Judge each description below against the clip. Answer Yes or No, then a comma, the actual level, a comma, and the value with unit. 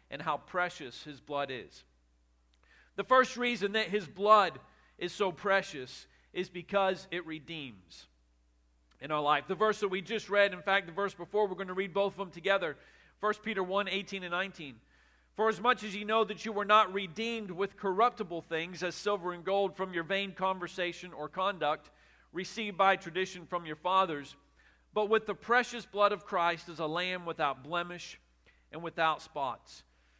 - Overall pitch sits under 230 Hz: Yes, medium, 185 Hz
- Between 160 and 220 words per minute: Yes, average, 185 wpm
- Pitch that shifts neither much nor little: Yes, average, 4.6 semitones